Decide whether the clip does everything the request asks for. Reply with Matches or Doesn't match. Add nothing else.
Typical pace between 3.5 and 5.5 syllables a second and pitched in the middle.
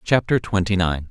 Doesn't match